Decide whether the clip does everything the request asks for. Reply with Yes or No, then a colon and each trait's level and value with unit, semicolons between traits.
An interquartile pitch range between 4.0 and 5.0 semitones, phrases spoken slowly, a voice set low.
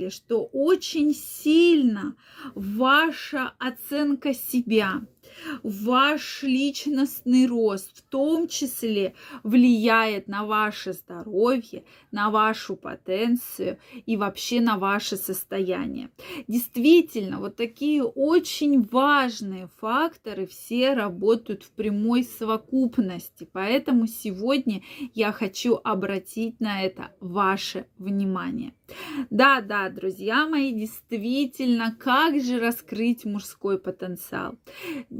No: average, 4.6 semitones; slow, 90 wpm; high, 235 Hz